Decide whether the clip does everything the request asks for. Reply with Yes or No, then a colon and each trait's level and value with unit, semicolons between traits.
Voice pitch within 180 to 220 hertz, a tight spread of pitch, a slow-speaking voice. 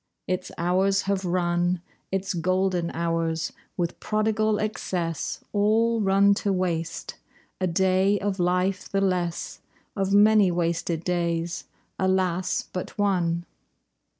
Yes: medium, 185 Hz; narrow, 2.3 semitones; slow, 115 wpm